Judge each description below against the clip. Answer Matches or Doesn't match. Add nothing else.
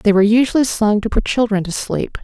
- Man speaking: Doesn't match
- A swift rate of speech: Matches